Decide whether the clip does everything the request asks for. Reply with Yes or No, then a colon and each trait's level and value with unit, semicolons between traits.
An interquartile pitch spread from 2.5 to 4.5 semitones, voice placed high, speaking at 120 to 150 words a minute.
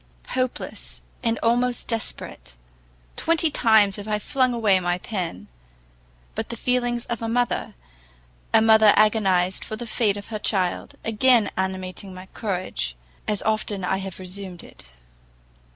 Yes: average, 3.7 semitones; high, 210 Hz; average, 140 wpm